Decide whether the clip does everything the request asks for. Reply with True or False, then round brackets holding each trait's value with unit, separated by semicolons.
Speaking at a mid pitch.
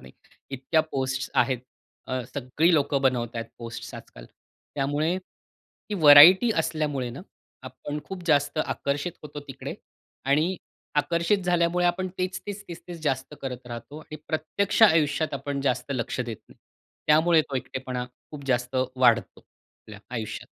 True (145 Hz)